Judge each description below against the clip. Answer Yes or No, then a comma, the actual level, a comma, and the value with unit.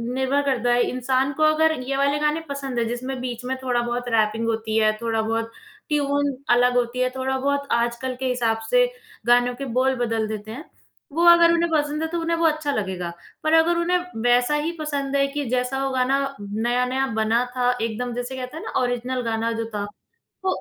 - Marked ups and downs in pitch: No, average, 3.2 semitones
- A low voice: No, very high, 255 Hz